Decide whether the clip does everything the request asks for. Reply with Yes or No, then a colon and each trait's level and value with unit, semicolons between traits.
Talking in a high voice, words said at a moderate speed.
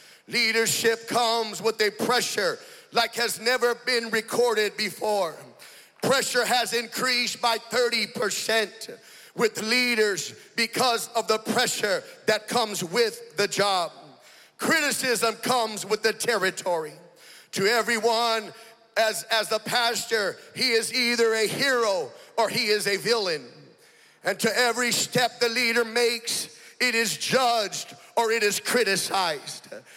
No: high, 230 Hz; slow, 125 wpm